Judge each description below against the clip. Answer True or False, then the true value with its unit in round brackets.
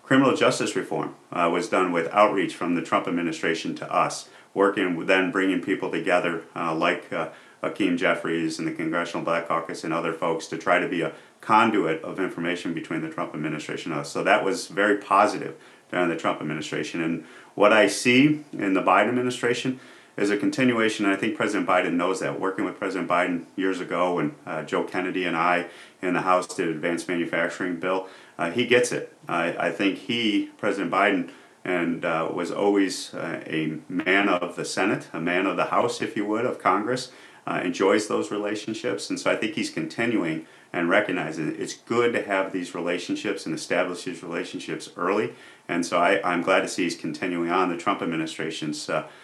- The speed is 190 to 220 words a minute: True (195 wpm)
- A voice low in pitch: True (95 Hz)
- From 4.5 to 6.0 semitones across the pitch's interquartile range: True (5.4 semitones)